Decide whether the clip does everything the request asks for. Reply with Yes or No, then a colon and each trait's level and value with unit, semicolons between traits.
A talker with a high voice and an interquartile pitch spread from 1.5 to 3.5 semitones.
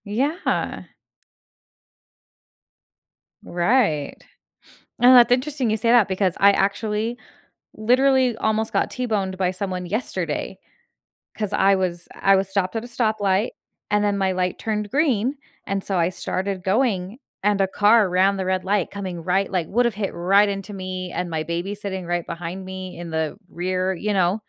Yes: high, 195 Hz; average, 2.9 semitones